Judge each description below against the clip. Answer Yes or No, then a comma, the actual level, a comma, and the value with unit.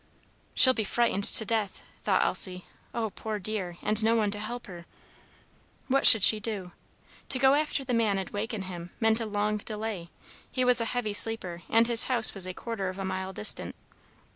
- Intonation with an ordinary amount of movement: Yes, average, 3.1 semitones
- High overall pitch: Yes, high, 215 Hz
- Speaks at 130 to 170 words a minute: No, average, 195 wpm